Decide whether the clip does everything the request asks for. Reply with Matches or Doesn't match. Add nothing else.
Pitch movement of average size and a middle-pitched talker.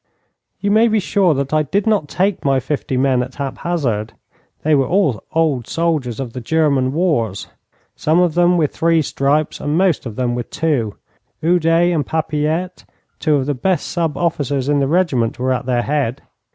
Matches